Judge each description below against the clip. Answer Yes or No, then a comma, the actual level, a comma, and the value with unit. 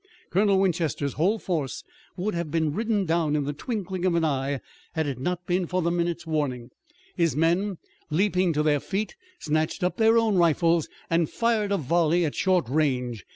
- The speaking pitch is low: No, medium, 170 Hz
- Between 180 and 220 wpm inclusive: Yes, average, 190 wpm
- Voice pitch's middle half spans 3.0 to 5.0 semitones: Yes, average, 3.7 semitones